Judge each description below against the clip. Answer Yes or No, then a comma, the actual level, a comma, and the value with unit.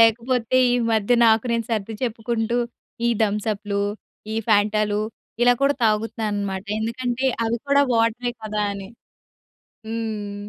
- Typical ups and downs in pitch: No, narrow, 2.0 semitones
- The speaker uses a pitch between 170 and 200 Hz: No, high, 220 Hz